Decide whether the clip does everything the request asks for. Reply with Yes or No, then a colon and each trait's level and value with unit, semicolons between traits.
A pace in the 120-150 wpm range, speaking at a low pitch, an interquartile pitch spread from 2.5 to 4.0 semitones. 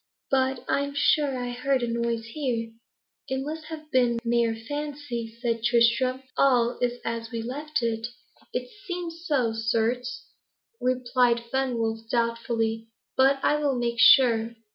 No: average, 140 wpm; high, 245 Hz; average, 2.8 semitones